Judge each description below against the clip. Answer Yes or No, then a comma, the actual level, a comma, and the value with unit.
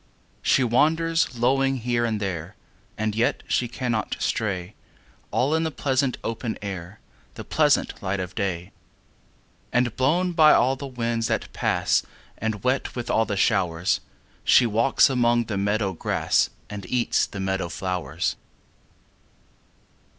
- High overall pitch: No, low, 115 Hz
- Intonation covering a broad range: No, average, 4.7 semitones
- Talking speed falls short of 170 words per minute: Yes, average, 140 wpm